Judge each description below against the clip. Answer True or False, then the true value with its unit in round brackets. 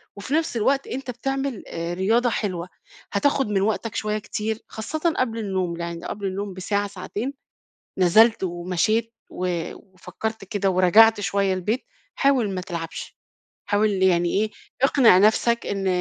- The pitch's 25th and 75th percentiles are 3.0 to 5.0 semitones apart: True (3.7 semitones)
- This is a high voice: True (205 Hz)